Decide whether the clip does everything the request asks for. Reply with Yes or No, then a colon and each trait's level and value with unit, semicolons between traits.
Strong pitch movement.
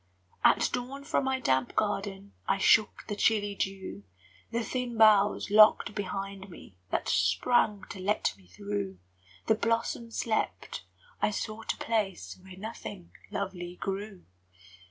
No: average, 2.8 semitones